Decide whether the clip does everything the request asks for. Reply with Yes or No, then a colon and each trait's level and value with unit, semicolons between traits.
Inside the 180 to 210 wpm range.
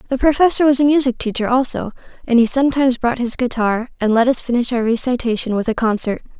Yes: fast, 205 wpm